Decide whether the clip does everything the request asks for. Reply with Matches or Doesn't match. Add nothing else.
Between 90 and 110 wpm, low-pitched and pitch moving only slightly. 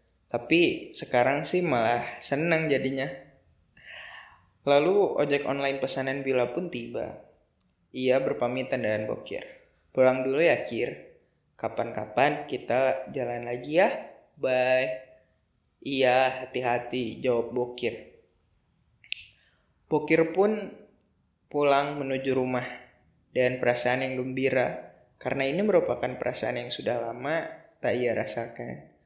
Matches